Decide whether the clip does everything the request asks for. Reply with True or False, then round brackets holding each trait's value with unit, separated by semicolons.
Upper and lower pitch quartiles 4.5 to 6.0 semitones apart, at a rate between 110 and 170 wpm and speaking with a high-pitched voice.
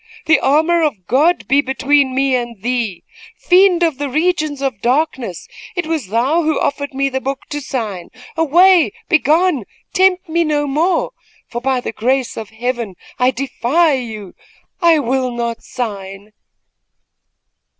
True (4.9 semitones; 150 wpm; 270 Hz)